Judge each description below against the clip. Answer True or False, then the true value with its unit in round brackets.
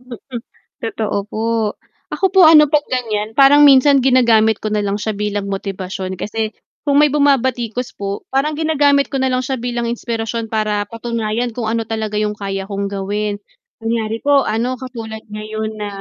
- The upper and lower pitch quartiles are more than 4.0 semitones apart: False (3.6 semitones)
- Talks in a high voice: True (225 Hz)